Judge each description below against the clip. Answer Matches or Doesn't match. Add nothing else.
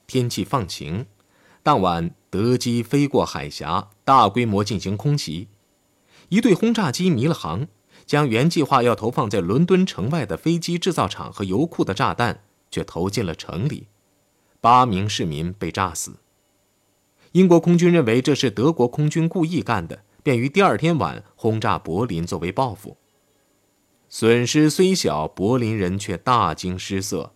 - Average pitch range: Doesn't match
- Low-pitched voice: Matches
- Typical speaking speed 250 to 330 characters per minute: Doesn't match